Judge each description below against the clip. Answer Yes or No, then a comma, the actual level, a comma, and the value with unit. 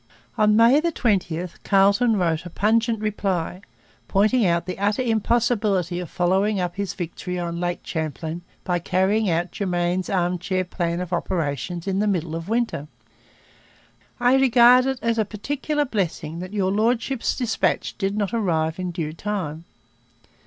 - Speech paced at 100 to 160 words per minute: Yes, average, 150 wpm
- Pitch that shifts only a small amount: No, average, 4.0 semitones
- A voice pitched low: No, high, 190 Hz